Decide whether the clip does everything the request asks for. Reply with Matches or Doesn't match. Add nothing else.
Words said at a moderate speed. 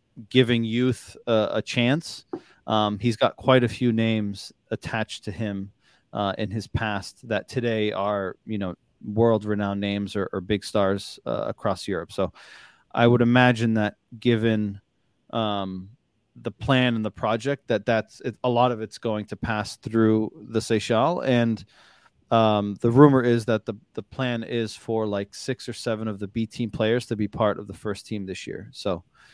Matches